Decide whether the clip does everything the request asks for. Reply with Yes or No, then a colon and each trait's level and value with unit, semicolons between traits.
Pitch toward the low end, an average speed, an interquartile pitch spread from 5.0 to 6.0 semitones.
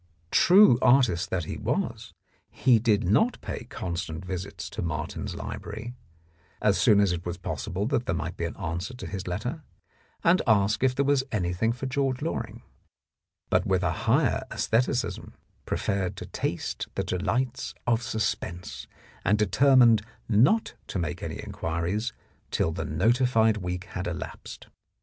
Yes: low, 105 Hz; average, 155 wpm; wide, 5.6 semitones